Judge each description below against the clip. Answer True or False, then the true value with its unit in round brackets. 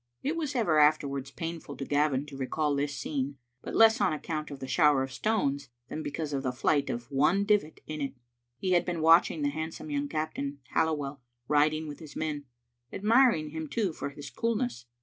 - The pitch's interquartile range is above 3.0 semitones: False (2.7 semitones)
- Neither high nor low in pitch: True (150 Hz)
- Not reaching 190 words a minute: False (200 wpm)